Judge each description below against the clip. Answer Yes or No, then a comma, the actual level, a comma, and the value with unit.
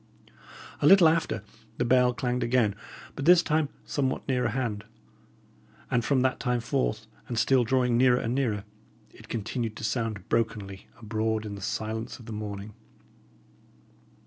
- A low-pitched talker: Yes, low, 120 Hz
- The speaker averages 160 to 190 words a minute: No, average, 150 wpm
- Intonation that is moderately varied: Yes, average, 3.1 semitones